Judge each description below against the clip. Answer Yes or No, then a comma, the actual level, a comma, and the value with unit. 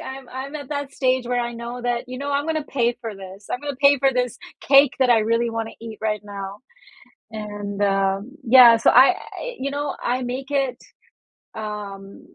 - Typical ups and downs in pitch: Yes, average, 4.1 semitones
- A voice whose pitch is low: No, high, 245 Hz